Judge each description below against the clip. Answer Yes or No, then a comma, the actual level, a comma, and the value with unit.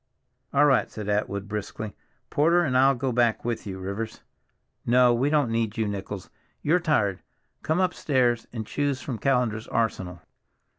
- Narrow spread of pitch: No, average, 4.5 semitones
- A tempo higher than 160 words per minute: No, average, 155 wpm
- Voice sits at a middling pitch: No, low, 120 Hz